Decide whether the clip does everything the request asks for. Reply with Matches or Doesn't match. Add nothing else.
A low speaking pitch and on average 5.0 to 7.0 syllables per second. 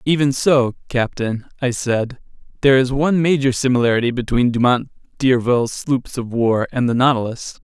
Matches